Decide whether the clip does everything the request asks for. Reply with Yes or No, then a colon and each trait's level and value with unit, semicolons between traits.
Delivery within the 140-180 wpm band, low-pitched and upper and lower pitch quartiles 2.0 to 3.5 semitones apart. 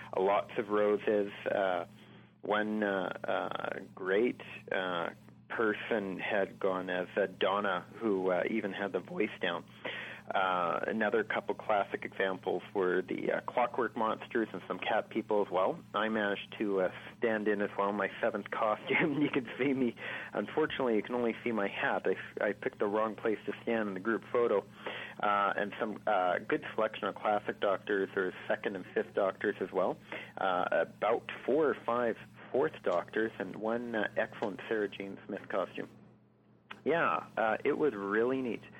Yes: average, 170 wpm; low, 105 Hz; narrow, 2.5 semitones